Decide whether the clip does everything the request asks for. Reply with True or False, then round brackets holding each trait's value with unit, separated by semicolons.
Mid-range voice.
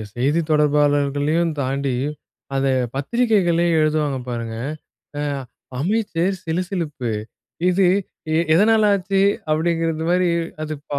True (160 Hz)